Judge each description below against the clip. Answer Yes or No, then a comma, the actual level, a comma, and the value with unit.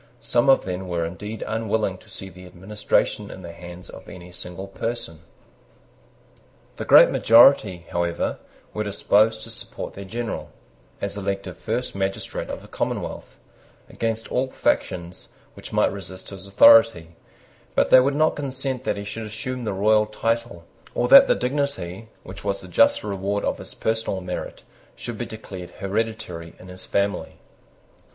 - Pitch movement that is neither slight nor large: Yes, average, 3.6 semitones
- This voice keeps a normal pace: Yes, average, 160 wpm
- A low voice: Yes, low, 100 Hz